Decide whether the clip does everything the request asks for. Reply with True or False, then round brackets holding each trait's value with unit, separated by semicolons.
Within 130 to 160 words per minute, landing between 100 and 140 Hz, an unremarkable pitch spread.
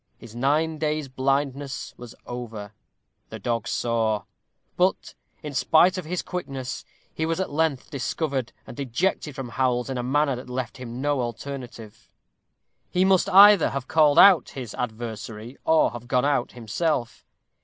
True (155 wpm; 135 Hz; 4.3 semitones)